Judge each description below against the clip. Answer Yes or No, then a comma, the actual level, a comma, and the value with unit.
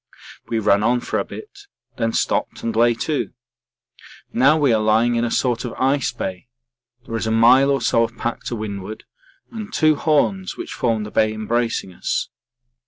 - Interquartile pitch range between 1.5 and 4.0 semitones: Yes, average, 3.7 semitones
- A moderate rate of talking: Yes, average, 185 wpm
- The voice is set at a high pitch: No, low, 120 Hz